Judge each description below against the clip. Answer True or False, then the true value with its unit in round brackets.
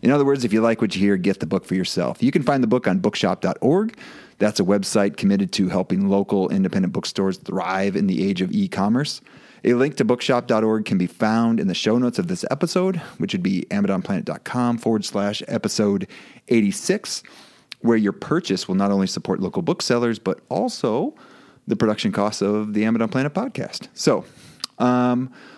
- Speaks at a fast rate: False (190 wpm)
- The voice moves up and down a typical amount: True (3.8 semitones)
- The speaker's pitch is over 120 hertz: False (110 Hz)